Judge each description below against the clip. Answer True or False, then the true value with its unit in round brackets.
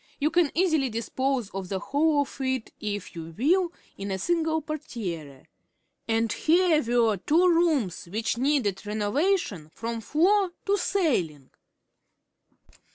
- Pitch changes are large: True (7.8 semitones)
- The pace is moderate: False (130 wpm)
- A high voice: True (260 Hz)